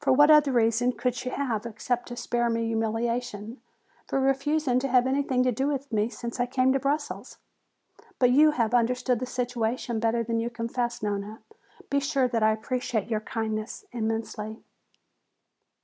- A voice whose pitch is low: No, high, 240 Hz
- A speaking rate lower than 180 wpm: Yes, average, 165 wpm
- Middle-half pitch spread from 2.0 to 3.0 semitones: Yes, narrow, 2.5 semitones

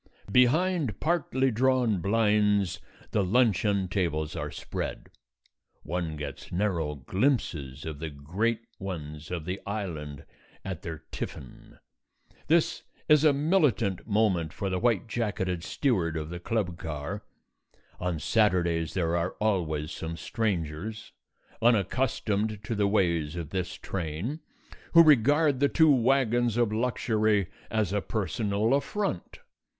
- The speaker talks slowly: Yes, slow, 125 wpm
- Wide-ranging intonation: Yes, wide, 5.7 semitones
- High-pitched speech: No, low, 100 Hz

